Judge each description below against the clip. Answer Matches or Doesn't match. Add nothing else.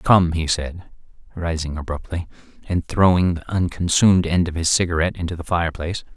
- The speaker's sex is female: Doesn't match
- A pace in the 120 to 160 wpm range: Matches